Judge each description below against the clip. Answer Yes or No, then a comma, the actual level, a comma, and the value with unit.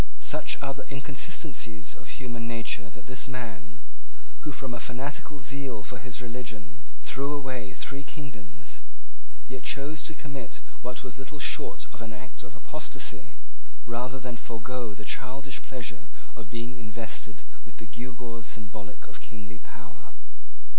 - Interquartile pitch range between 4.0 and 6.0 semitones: No, average, 3.2 semitones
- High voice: No, low, 120 Hz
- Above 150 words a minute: No, average, 145 wpm